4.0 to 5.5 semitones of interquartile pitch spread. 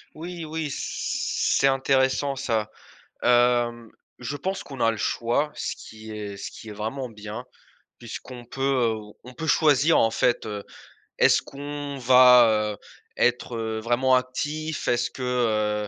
No: average, 3.6 semitones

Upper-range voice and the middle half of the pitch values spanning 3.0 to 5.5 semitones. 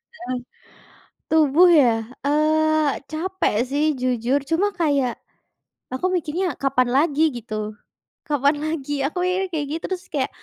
Yes: very high, 295 Hz; average, 3.8 semitones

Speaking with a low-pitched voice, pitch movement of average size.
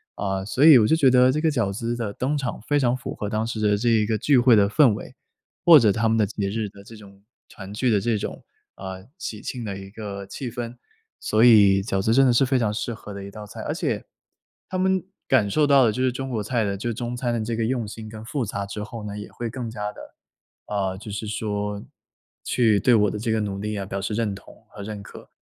Yes: low, 110 Hz; average, 3.0 semitones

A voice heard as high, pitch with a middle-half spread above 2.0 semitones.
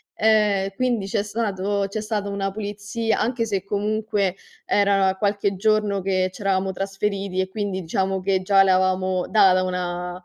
No: high, 195 Hz; narrow, 1.7 semitones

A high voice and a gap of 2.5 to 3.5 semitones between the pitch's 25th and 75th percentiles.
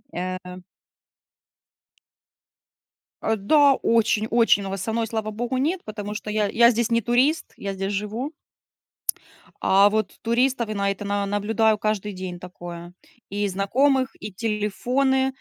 Yes: high, 215 Hz; average, 3.0 semitones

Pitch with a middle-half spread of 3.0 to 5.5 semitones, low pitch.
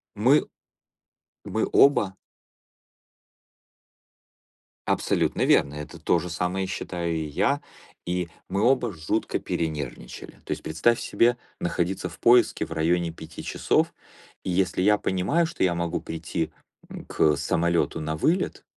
Yes: average, 3.6 semitones; very low, 90 Hz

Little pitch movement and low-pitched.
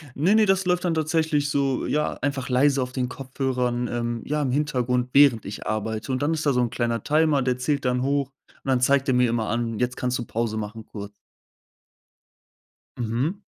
No: average, 3.3 semitones; low, 130 Hz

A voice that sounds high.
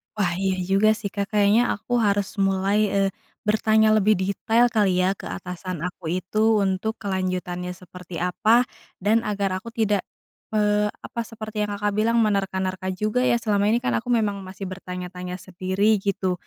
Yes: high, 200 Hz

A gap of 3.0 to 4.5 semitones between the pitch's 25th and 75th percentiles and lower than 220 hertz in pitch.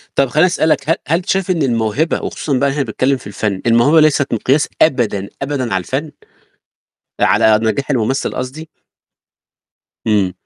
No: average, 5.2 semitones; low, 135 Hz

